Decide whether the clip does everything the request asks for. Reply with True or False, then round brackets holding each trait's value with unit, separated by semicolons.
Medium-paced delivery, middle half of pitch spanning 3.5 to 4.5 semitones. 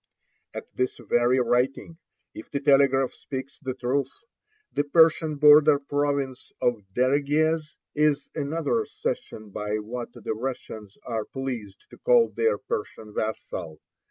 False (130 wpm; 3.9 semitones)